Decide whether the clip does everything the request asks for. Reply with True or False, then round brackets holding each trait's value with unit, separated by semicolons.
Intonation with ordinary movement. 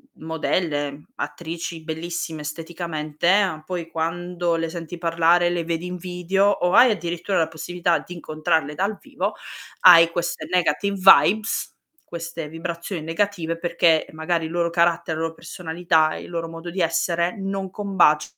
False (1.6 semitones)